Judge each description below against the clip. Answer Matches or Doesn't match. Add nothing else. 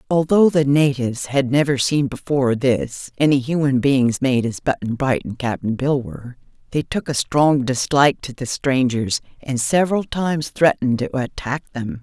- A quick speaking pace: Doesn't match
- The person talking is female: Matches